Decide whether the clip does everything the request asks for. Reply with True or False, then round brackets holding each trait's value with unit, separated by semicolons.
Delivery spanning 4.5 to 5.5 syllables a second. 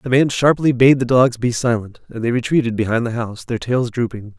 False (5.7 syllables/s)